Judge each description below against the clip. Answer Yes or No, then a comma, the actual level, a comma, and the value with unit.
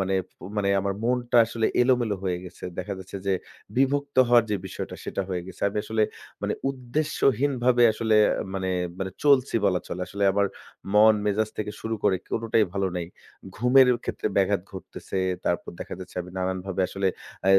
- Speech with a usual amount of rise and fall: Yes, average, 4.2 semitones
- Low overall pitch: Yes, low, 105 Hz